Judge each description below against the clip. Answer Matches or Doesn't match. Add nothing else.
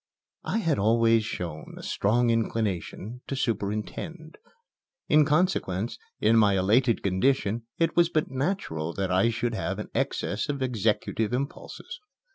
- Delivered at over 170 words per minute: Doesn't match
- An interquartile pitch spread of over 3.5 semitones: Matches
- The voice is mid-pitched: Doesn't match